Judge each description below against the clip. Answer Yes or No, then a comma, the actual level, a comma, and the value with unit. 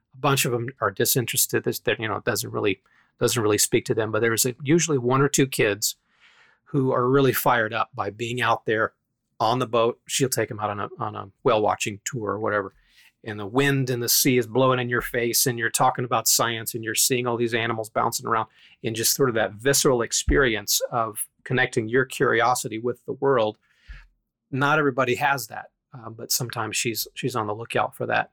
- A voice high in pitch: No, low, 125 Hz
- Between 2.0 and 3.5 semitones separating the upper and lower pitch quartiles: Yes, average, 2.7 semitones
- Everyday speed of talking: No, fast, 215 wpm